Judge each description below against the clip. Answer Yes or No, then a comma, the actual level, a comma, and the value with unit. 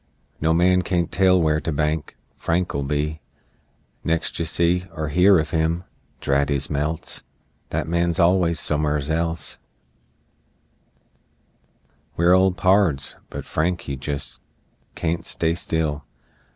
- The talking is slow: Yes, slow, 125 wpm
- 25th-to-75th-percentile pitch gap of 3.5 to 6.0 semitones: No, narrow, 2.5 semitones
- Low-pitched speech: Yes, very low, 80 Hz